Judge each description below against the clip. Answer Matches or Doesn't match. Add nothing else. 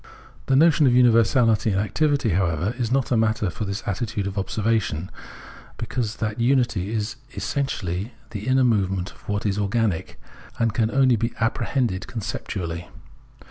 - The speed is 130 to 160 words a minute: Matches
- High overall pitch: Doesn't match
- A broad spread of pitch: Doesn't match